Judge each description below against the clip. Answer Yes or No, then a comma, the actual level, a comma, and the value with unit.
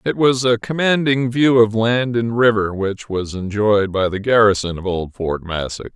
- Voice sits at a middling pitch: No, low, 110 Hz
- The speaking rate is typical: Yes, average, 190 wpm